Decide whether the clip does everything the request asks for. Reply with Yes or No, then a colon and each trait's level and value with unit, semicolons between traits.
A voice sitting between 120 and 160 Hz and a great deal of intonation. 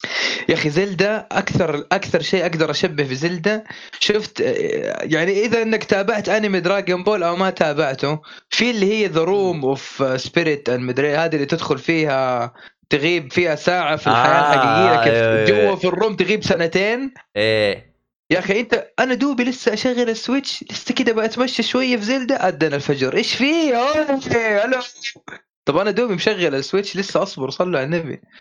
No: high, 195 Hz; wide, 7.0 semitones